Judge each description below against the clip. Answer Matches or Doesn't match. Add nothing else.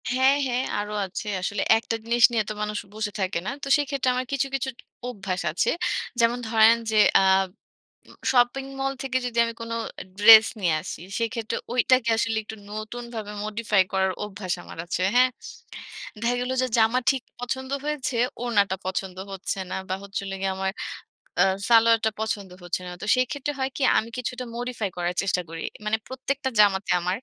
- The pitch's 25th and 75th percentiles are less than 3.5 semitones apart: Doesn't match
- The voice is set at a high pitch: Matches